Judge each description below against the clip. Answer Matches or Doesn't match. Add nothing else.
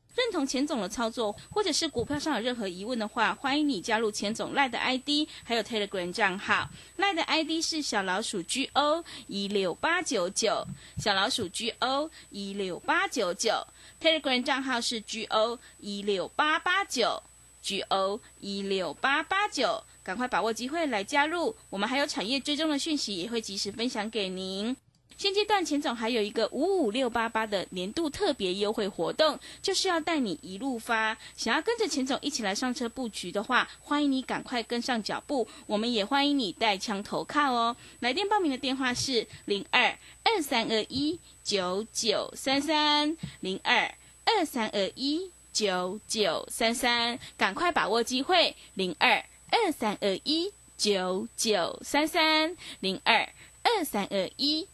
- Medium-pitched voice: Doesn't match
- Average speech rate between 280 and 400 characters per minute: Doesn't match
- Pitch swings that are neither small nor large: Doesn't match